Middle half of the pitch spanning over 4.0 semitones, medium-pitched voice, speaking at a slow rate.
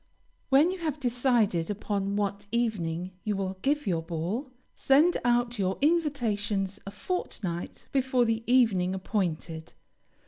No: wide, 5.4 semitones; high, 210 Hz; slow, 130 wpm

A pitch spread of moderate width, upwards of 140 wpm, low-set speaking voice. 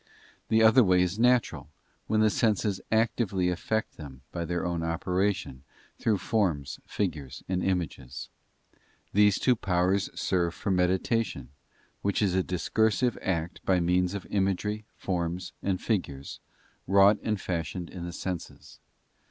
No: average, 3.1 semitones; slow, 135 wpm; very low, 95 Hz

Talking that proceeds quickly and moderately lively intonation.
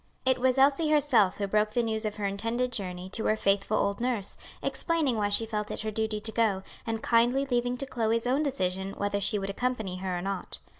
Yes: fast, 220 wpm; average, 3.7 semitones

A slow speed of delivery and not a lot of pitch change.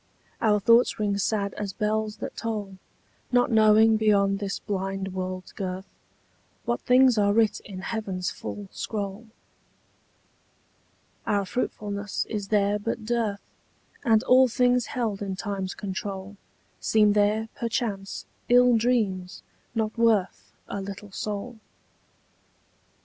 Yes: slow, 120 wpm; narrow, 2.3 semitones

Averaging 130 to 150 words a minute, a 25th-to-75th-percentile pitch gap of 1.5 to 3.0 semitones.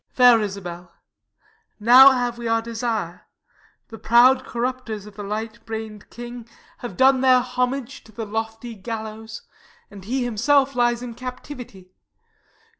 Yes: average, 140 wpm; narrow, 2.5 semitones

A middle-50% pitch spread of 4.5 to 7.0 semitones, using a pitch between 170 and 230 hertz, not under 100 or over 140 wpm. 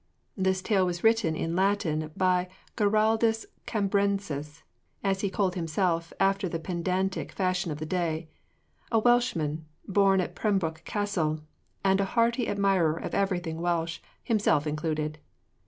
No: average, 3.6 semitones; medium, 185 Hz; slow, 135 wpm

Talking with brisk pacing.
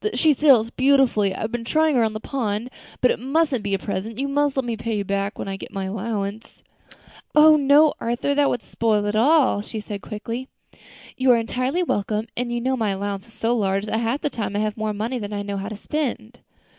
Yes: fast, 230 wpm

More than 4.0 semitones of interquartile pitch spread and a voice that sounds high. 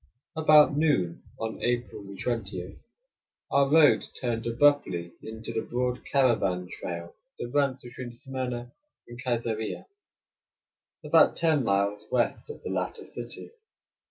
No: average, 4.4 semitones; low, 120 Hz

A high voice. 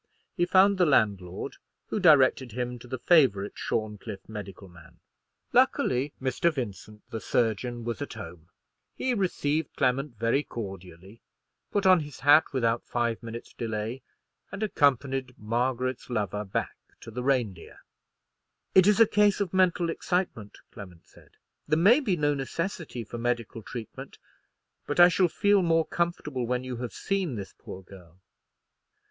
No: low, 125 Hz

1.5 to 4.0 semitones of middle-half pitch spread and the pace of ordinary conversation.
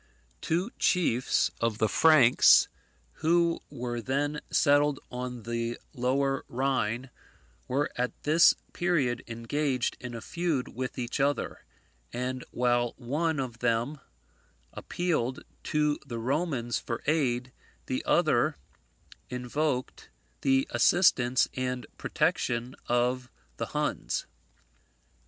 No: average, 3.4 semitones; slow, 105 wpm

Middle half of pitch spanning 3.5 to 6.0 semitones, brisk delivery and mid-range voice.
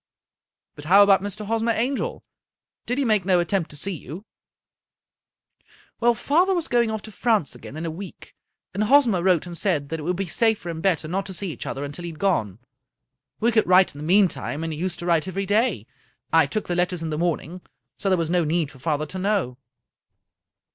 Yes: average, 4.5 semitones; fast, 225 wpm; medium, 180 Hz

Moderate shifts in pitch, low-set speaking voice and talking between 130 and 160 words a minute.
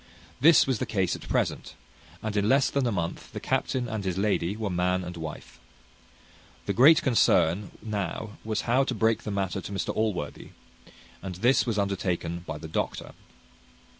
No: average, 4.1 semitones; low, 105 Hz; average, 170 wpm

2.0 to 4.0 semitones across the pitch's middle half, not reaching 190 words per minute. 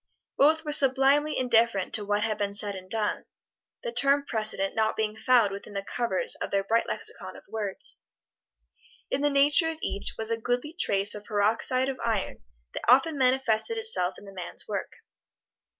No: average, 4.9 semitones; average, 180 wpm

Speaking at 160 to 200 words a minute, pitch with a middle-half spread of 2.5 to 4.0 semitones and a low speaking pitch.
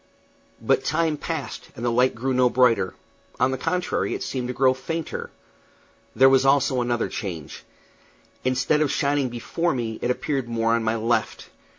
Yes: average, 170 wpm; average, 2.9 semitones; low, 130 Hz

